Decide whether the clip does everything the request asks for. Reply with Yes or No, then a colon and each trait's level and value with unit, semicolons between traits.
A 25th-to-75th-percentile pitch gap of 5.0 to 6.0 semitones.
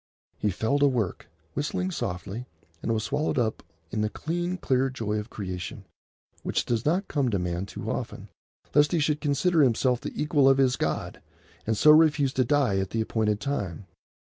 Yes: wide, 5.5 semitones